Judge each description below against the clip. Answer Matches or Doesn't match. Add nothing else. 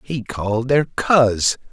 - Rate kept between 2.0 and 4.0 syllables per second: Matches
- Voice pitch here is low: Matches